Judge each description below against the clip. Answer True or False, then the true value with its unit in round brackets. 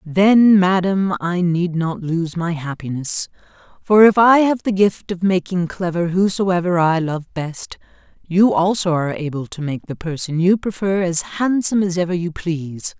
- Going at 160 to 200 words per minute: True (170 wpm)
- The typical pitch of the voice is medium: True (180 Hz)